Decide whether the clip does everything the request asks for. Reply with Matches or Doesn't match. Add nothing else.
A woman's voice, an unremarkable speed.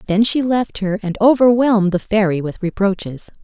Matches